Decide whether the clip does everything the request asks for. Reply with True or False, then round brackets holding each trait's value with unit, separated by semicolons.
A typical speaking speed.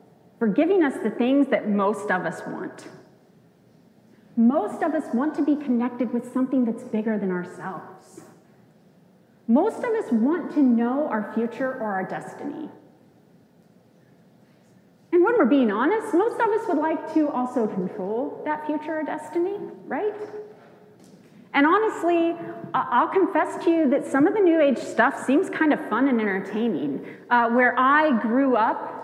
True (155 wpm)